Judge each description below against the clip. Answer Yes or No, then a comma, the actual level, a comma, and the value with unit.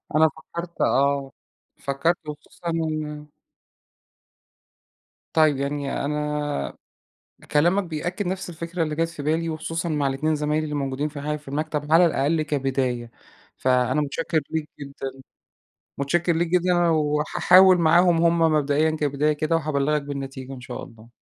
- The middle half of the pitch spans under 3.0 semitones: Yes, narrow, 2.6 semitones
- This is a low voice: No, medium, 150 Hz